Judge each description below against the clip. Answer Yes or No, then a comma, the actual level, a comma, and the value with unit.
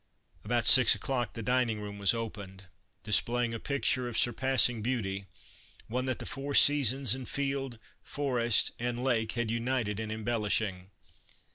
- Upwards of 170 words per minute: No, average, 145 wpm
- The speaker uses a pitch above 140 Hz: No, low, 120 Hz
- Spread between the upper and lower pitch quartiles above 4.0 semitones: No, average, 2.9 semitones